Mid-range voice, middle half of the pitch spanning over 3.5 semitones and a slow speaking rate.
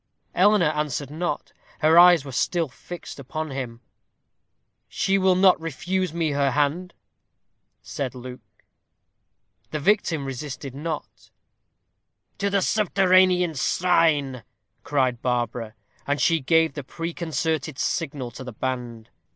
Yes: medium, 155 Hz; average, 5.0 semitones; slow, 120 wpm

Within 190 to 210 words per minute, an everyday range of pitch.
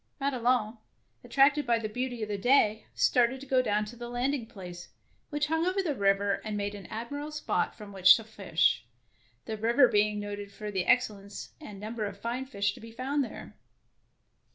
Yes: average, 195 wpm; average, 4.0 semitones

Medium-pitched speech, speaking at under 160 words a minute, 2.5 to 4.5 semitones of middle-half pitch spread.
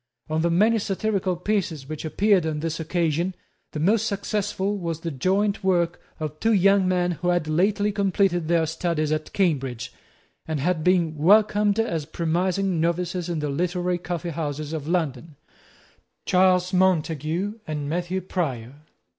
Yes: medium, 175 Hz; average, 150 wpm; average, 3.3 semitones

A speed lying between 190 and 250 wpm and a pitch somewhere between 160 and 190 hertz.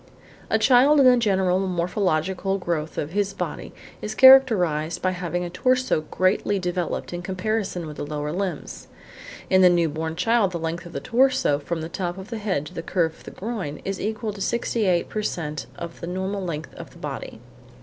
Yes: average, 200 wpm; medium, 185 Hz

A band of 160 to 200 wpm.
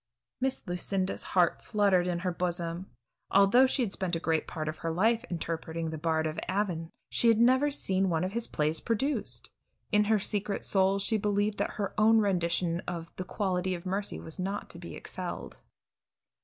Yes: average, 190 wpm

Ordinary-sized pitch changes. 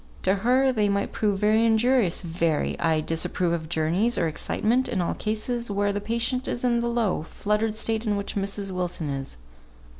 Yes: average, 4.7 semitones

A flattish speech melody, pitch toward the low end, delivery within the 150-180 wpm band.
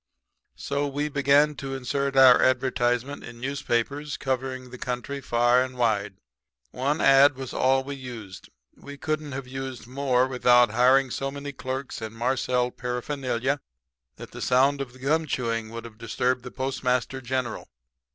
Yes: narrow, 2.0 semitones; low, 130 Hz; average, 155 wpm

